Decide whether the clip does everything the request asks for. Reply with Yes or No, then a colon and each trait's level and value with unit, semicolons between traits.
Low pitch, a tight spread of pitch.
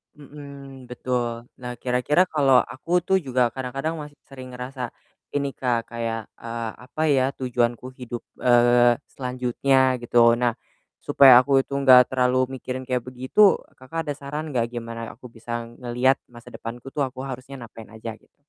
Yes: low, 125 Hz; narrow, 2.2 semitones